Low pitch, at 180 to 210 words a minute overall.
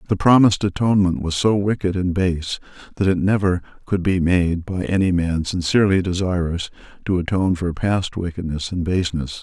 No: very low, 90 Hz; average, 165 wpm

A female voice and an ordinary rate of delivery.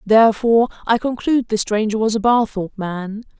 Yes: female; average, 160 wpm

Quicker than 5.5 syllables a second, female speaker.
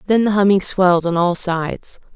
No: 5.4 syllables/s; female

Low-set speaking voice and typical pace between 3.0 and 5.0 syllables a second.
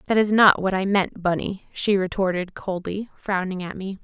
No: high, 190 Hz; 4.9 syllables/s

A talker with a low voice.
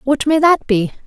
No: very high, 270 Hz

